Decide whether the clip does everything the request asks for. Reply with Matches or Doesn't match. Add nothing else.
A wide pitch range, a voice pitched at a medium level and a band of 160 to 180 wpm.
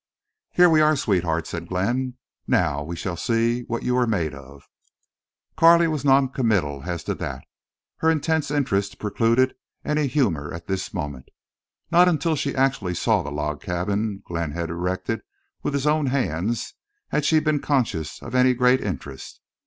Doesn't match